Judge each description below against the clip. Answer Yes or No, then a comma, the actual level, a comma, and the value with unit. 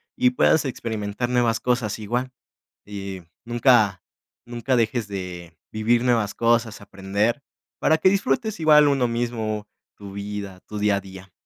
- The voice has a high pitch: No, low, 115 Hz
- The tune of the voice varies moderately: Yes, average, 3.4 semitones